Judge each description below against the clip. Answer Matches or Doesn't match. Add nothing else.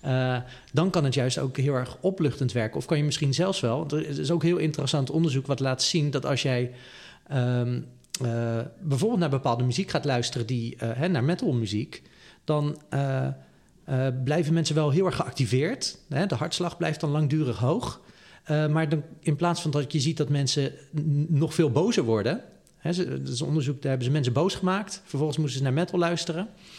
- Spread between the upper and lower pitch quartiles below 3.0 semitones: Doesn't match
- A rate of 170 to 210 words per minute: Matches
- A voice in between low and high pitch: Matches